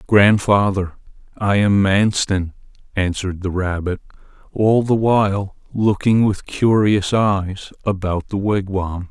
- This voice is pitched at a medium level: No, low, 100 Hz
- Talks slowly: Yes, slow, 110 wpm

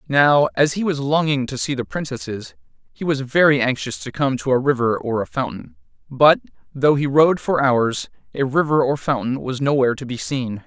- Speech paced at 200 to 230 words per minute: Yes, fast, 205 wpm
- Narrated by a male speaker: Yes, male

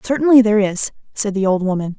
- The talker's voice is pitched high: Yes, high, 210 Hz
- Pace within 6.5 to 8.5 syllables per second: Yes, 6.6 syllables/s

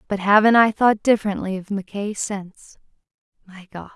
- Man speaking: No, female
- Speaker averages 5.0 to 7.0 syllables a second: Yes, 5.3 syllables/s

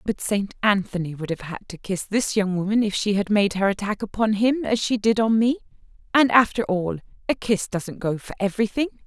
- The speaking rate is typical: No, fast, 210 wpm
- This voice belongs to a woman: Yes, female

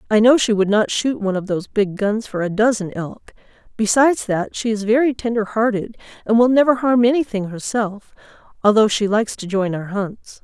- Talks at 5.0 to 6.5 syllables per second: Yes, 5.5 syllables/s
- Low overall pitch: No, high, 215 Hz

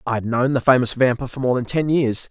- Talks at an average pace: No, fast, 285 wpm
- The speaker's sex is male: Yes, male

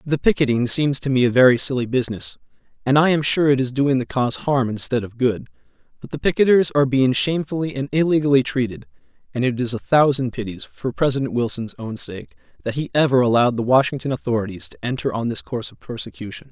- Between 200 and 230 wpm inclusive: Yes, fast, 205 wpm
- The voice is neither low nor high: No, low, 130 Hz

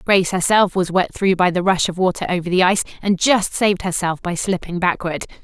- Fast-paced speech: Yes, fast, 220 wpm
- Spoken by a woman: Yes, female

